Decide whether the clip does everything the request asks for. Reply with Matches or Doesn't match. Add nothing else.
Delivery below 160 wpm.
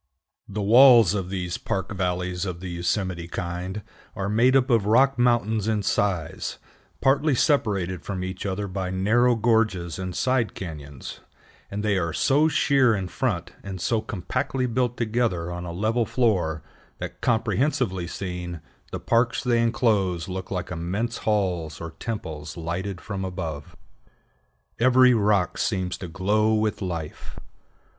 Matches